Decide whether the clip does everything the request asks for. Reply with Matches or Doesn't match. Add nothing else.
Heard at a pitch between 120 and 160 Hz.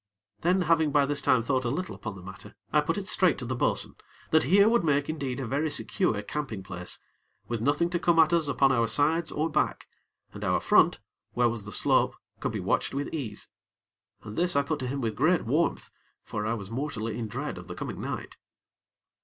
Matches